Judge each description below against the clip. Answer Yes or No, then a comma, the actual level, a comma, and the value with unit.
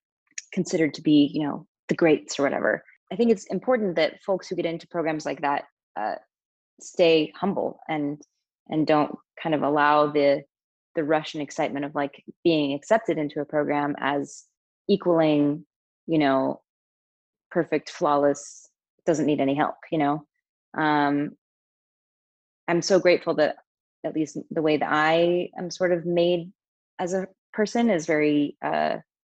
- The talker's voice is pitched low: No, medium, 155 Hz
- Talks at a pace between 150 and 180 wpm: Yes, average, 155 wpm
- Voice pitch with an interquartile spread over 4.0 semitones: No, average, 3.1 semitones